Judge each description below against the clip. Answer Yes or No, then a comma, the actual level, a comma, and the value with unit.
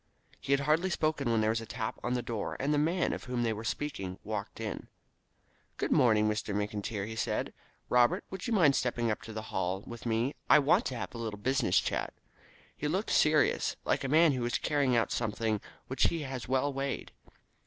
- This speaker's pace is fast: Yes, fast, 215 wpm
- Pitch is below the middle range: Yes, low, 120 Hz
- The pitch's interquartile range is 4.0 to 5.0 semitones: Yes, average, 4.6 semitones